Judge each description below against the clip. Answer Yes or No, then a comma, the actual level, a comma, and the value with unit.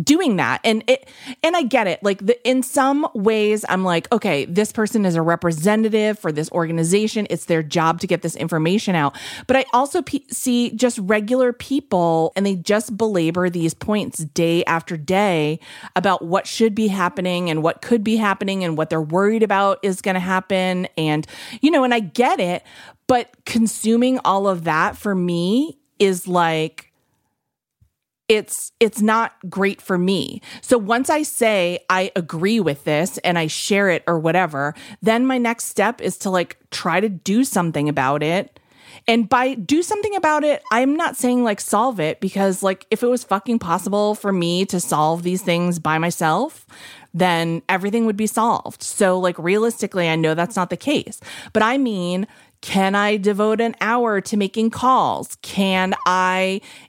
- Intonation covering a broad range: No, average, 4.8 semitones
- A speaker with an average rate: Yes, average, 180 wpm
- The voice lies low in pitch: No, high, 200 Hz